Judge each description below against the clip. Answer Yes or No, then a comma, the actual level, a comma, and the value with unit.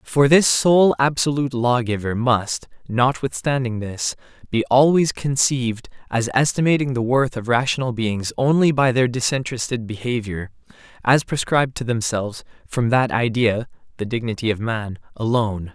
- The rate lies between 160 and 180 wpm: No, slow, 135 wpm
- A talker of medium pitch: No, low, 120 Hz